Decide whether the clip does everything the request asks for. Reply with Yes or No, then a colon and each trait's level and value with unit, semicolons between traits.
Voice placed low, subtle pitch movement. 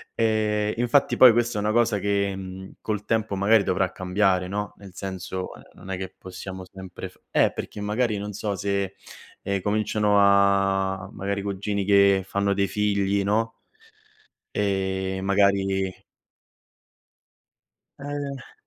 Yes: low, 100 Hz; narrow, 1.6 semitones